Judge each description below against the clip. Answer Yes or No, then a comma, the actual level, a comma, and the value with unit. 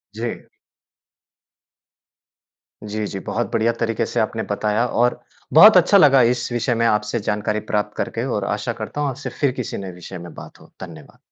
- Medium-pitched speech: No, low, 110 Hz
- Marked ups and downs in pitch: No, average, 2.7 semitones